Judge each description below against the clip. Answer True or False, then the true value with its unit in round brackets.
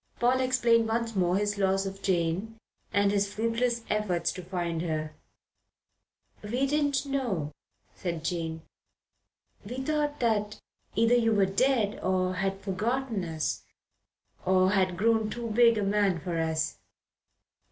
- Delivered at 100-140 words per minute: True (135 wpm)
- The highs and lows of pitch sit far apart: False (4.2 semitones)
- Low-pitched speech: False (205 Hz)